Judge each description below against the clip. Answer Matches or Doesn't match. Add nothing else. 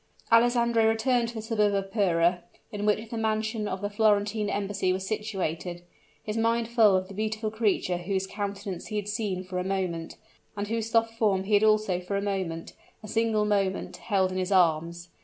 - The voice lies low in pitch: Doesn't match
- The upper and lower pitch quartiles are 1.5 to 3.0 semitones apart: Matches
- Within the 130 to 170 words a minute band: Doesn't match